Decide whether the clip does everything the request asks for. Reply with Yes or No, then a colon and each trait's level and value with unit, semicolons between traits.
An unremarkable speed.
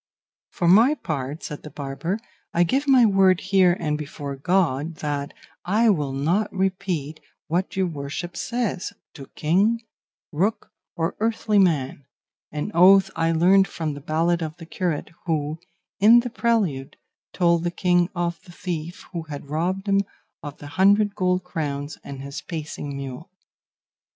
Yes: average, 155 wpm